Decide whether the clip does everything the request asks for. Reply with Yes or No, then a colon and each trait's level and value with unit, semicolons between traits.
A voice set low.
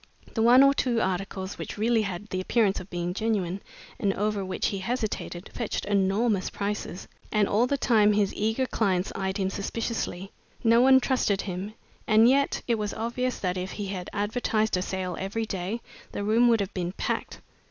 No: high, 205 Hz